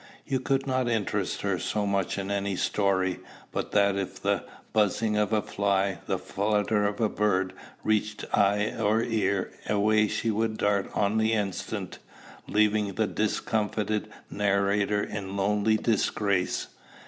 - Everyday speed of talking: Yes, average, 145 wpm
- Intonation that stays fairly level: Yes, narrow, 1.4 semitones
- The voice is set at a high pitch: No, low, 105 Hz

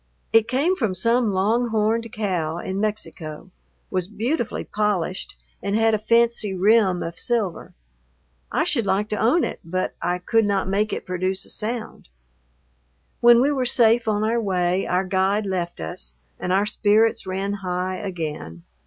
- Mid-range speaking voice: No, high, 205 Hz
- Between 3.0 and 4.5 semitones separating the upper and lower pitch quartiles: Yes, average, 3.5 semitones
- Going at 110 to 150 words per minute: No, average, 160 wpm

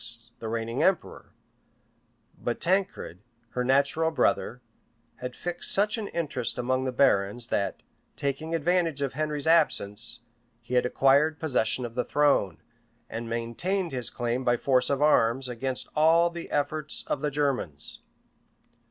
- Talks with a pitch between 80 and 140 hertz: Yes, low, 135 Hz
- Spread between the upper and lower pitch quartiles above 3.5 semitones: Yes, average, 4.7 semitones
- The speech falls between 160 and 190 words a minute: No, average, 140 wpm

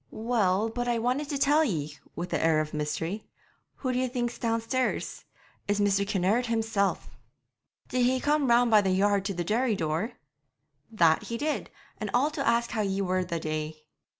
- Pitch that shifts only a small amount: No, average, 5.0 semitones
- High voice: Yes, high, 215 Hz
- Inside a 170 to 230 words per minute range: Yes, average, 180 wpm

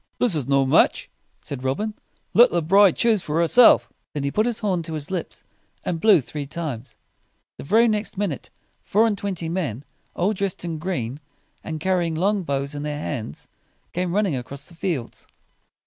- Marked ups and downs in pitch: Yes, wide, 5.8 semitones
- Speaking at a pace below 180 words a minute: No, average, 190 wpm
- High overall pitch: No, medium, 170 Hz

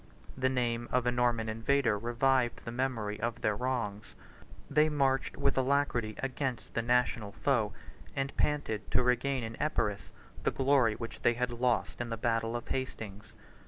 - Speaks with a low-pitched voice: Yes, low, 120 Hz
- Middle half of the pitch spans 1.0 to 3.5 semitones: Yes, average, 2.7 semitones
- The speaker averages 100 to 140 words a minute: No, average, 165 wpm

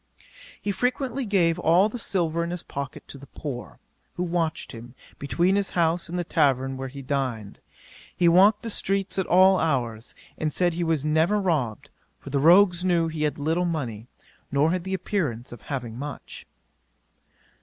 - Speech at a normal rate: Yes, average, 175 wpm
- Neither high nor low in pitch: Yes, medium, 165 Hz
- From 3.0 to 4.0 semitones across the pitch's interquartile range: No, average, 4.8 semitones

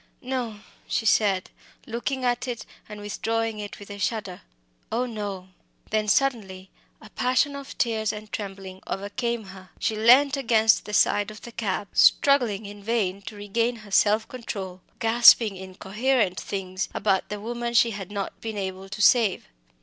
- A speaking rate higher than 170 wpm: No, average, 160 wpm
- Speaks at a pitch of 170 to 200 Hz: No, high, 215 Hz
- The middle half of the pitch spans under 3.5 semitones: Yes, average, 3.1 semitones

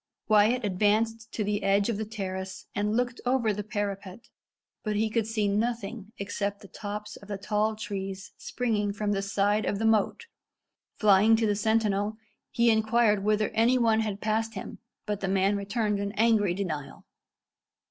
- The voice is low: No, high, 210 Hz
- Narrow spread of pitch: Yes, narrow, 1.8 semitones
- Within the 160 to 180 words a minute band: Yes, average, 170 wpm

